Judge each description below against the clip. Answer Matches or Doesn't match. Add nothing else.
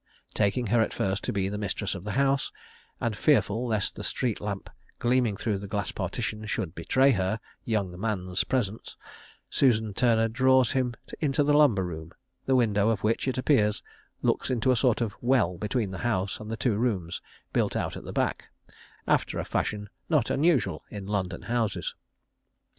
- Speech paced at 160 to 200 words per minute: Matches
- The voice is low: Matches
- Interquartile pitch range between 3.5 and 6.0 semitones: Matches